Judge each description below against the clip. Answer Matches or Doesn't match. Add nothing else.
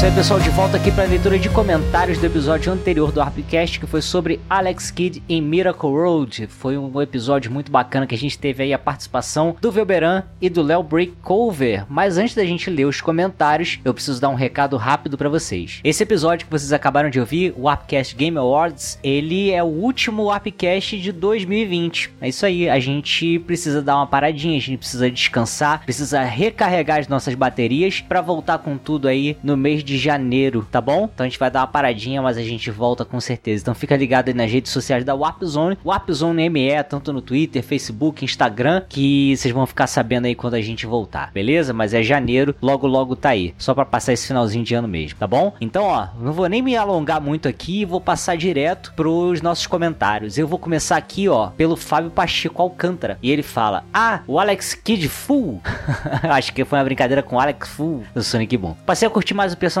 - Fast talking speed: Matches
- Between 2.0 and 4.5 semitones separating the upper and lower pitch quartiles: Doesn't match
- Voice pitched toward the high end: Doesn't match